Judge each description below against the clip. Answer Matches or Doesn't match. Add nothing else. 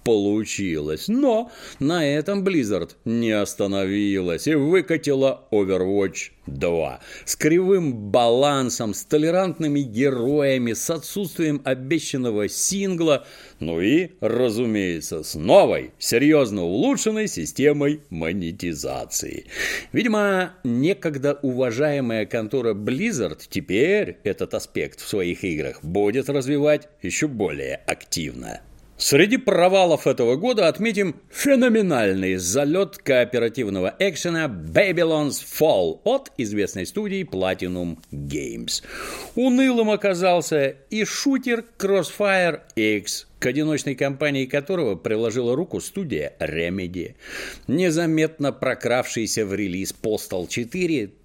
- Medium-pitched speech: Matches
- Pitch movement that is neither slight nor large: Doesn't match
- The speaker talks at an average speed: Doesn't match